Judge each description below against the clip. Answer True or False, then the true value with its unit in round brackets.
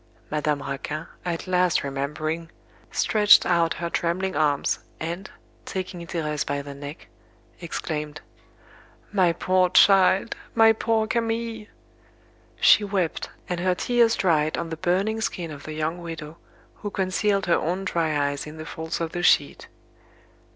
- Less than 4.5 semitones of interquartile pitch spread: True (3.8 semitones)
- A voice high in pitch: False (170 Hz)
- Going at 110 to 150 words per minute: True (145 wpm)